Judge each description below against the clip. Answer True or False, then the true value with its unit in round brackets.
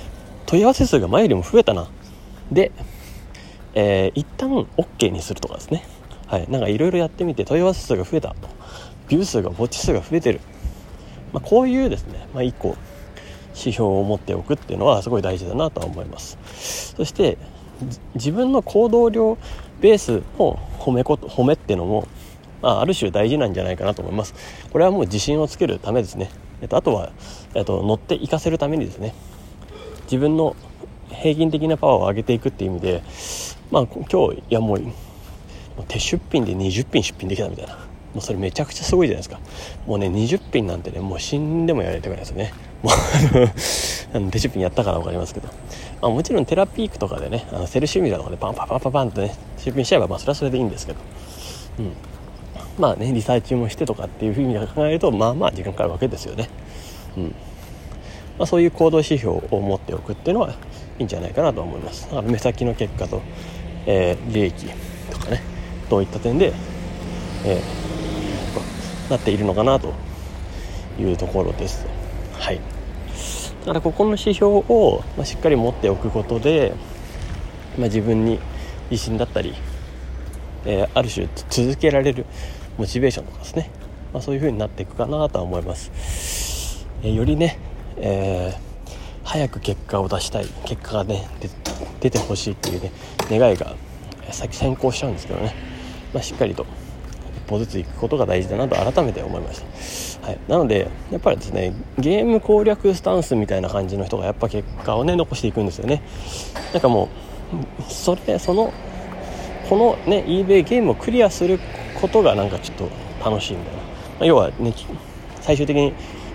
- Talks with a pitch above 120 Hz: False (105 Hz)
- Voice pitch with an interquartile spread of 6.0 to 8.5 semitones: True (6.5 semitones)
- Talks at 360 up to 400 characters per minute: True (370 characters per minute)